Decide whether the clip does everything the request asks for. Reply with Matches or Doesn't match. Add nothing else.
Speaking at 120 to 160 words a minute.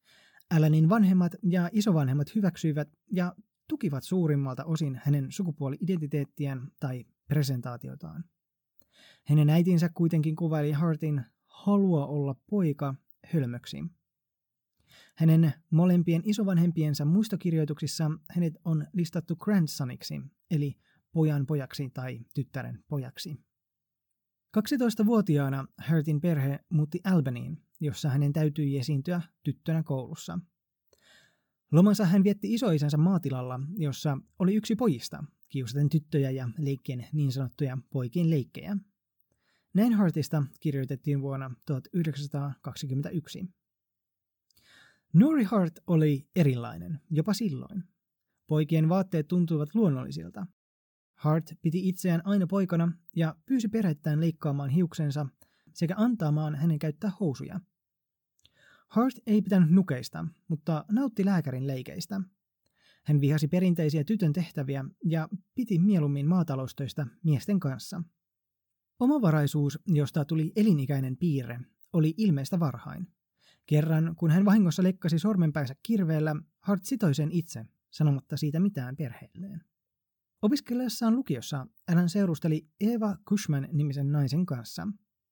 Doesn't match